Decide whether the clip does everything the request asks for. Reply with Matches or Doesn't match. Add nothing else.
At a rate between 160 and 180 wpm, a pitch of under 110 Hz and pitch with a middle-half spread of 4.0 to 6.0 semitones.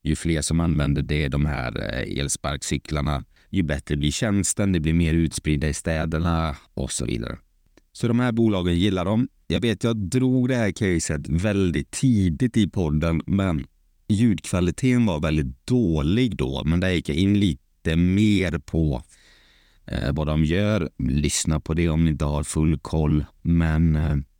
Matches